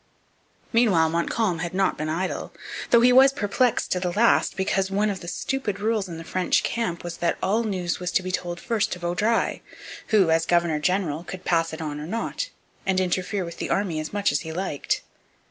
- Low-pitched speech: No, medium, 185 Hz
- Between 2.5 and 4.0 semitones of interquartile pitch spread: Yes, average, 3.4 semitones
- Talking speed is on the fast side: Yes, fast, 210 wpm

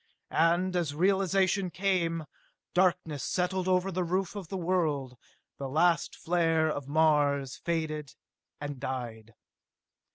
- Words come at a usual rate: No, slow, 120 wpm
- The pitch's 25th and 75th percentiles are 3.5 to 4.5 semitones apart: Yes, average, 3.9 semitones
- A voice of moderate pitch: Yes, medium, 165 Hz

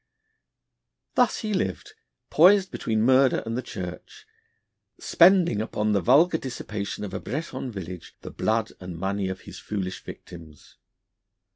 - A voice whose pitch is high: No, low, 110 Hz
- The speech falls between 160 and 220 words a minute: No, slow, 135 wpm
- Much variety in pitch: Yes, wide, 6.6 semitones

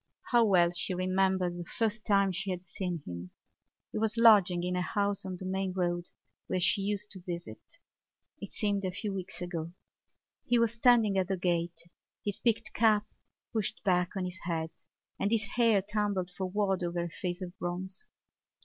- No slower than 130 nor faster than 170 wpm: No, average, 180 wpm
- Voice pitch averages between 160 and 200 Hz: Yes, high, 190 Hz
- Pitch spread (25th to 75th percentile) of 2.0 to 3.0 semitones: Yes, average, 2.7 semitones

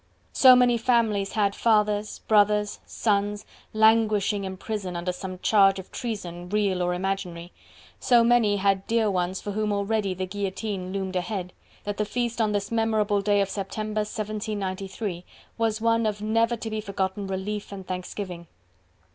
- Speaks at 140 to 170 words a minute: Yes, average, 155 wpm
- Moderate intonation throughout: No, narrow, 2.3 semitones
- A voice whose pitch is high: Yes, high, 205 Hz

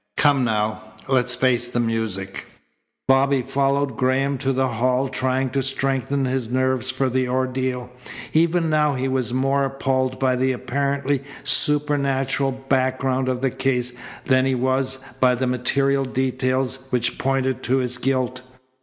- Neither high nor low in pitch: No, low, 130 Hz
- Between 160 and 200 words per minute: No, average, 145 wpm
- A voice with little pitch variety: Yes, narrow, 1.2 semitones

